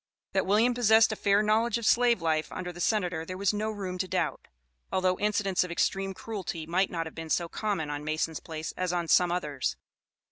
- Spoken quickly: Yes, fast, 210 wpm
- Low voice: No, medium, 185 Hz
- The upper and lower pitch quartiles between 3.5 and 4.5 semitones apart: Yes, average, 4.0 semitones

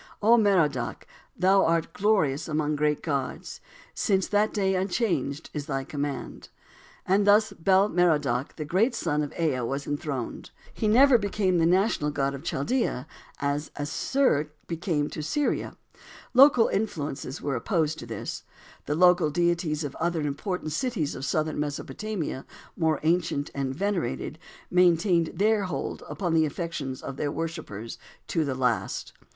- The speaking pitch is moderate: Yes, medium, 160 Hz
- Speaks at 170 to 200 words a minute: No, average, 145 wpm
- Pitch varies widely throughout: No, average, 4.9 semitones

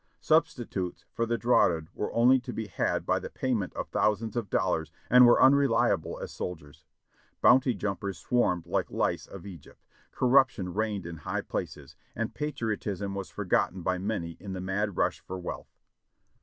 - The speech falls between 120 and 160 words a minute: No, average, 170 wpm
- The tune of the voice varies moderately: Yes, average, 4.5 semitones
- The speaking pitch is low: Yes, low, 100 Hz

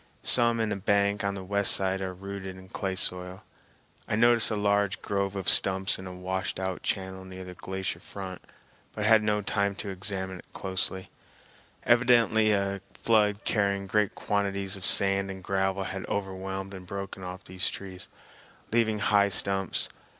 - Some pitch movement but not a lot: No, narrow, 1.4 semitones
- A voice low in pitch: Yes, low, 100 Hz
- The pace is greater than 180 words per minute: No, average, 165 wpm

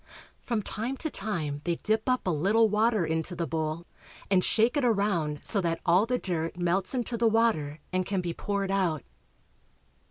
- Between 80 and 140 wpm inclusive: No, average, 185 wpm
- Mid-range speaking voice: No, high, 195 Hz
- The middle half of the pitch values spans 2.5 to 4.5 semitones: No, average, 5.0 semitones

